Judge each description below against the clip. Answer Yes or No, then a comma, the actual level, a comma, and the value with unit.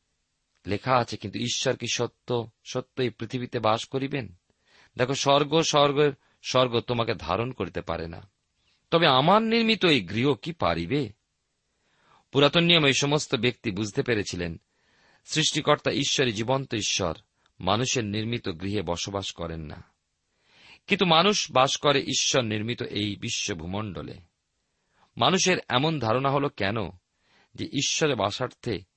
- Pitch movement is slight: No, wide, 5.6 semitones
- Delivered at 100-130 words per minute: Yes, fast, 120 wpm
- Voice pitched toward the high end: No, low, 120 Hz